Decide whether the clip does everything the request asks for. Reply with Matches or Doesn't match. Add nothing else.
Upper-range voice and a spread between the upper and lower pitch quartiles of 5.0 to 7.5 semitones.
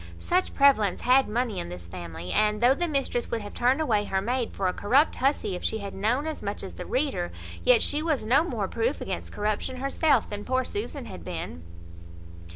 Matches